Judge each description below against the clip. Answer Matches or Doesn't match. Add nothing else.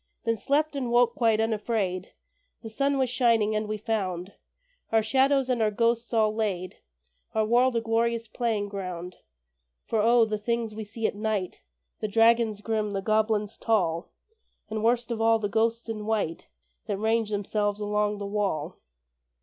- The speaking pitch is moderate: Doesn't match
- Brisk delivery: Doesn't match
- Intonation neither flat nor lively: Doesn't match